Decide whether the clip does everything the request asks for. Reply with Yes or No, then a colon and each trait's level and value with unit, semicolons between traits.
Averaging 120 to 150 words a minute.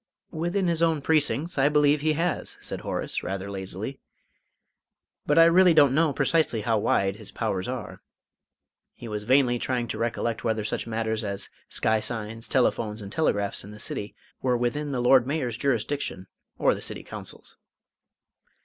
No: average, 165 wpm